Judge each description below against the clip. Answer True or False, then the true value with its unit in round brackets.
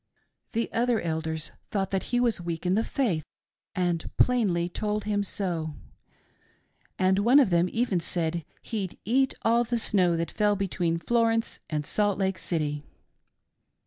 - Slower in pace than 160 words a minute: True (150 wpm)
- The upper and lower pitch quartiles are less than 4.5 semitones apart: False (5.0 semitones)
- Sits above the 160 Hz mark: True (190 Hz)